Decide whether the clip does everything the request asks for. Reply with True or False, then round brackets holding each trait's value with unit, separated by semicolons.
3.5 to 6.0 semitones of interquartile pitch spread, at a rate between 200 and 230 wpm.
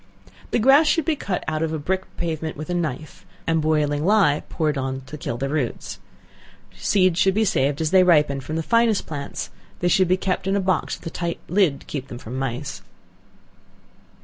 True (4.5 semitones; 205 wpm)